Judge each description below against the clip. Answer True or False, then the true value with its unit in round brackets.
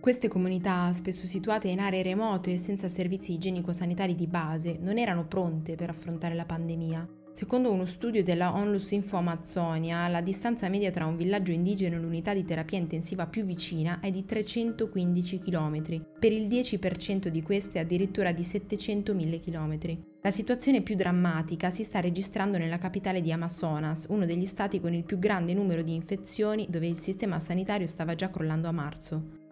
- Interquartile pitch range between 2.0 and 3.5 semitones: True (3.0 semitones)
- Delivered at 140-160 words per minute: False (170 wpm)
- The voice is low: False (180 Hz)